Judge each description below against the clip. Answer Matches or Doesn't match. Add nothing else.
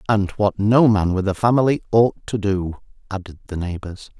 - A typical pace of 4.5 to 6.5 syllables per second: Matches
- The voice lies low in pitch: Matches